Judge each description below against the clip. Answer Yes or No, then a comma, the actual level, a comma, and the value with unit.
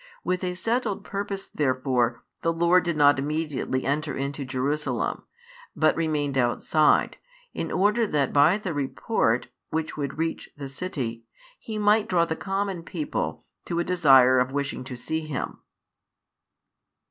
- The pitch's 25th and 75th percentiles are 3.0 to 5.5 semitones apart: Yes, average, 4.9 semitones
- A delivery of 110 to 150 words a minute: Yes, average, 145 wpm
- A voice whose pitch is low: No, medium, 155 Hz